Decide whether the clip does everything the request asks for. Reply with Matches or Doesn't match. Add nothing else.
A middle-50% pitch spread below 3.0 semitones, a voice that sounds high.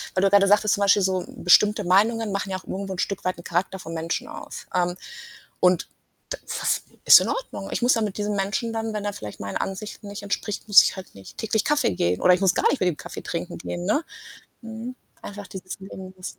Matches